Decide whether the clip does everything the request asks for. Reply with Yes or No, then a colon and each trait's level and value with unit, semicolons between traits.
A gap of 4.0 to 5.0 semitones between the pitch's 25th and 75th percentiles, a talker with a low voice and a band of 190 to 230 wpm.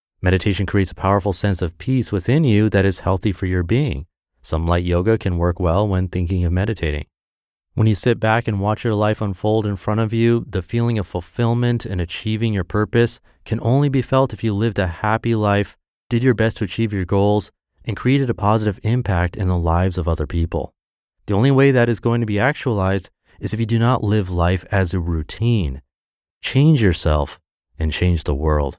Yes: average, 4.3 semitones; low, 100 Hz; fast, 205 wpm